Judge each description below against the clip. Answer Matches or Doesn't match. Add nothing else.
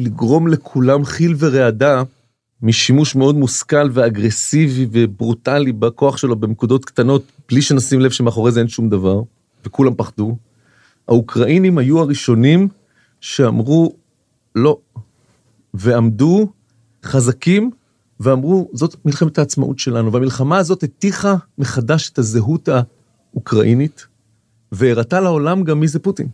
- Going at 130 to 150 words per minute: Doesn't match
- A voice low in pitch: Matches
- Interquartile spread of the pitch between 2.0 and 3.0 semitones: Doesn't match